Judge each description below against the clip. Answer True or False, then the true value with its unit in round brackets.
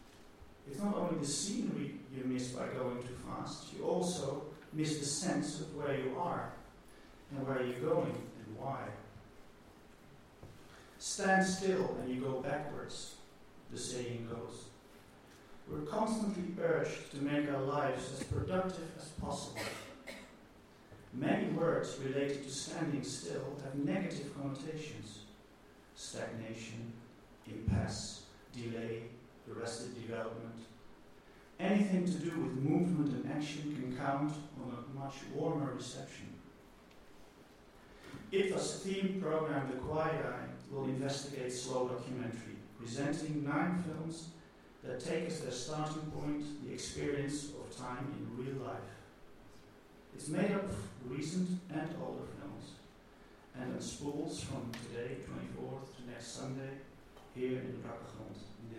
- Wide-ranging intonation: False (4.7 semitones)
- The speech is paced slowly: True (125 wpm)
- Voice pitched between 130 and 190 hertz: True (135 Hz)